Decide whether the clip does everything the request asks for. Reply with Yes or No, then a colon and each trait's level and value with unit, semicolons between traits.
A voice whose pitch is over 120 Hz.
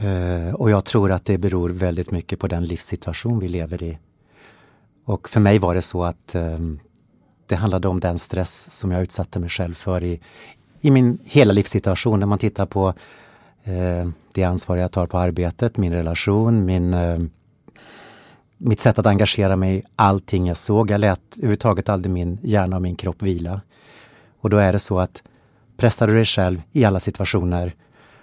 No: very low, 95 Hz